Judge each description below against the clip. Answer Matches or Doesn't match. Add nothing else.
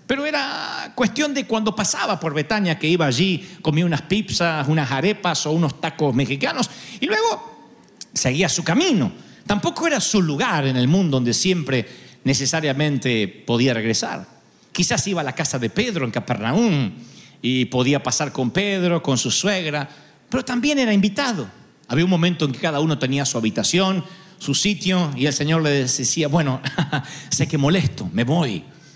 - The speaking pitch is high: Doesn't match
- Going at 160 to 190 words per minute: Matches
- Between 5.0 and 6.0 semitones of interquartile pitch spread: Matches